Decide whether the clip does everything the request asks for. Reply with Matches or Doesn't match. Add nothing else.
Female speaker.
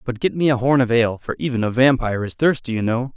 Doesn't match